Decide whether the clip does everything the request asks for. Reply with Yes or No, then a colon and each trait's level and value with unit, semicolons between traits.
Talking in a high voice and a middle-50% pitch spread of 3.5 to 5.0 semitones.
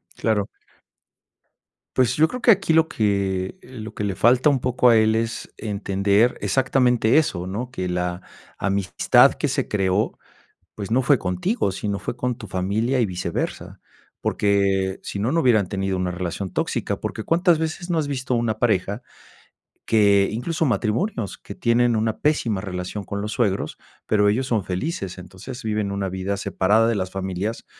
No: low, 105 Hz; average, 4.3 semitones